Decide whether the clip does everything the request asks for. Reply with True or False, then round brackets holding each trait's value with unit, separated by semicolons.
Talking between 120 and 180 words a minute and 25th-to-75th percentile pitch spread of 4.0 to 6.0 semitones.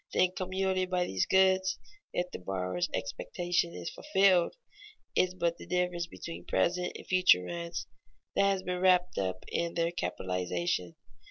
True (155 wpm; 4.8 semitones)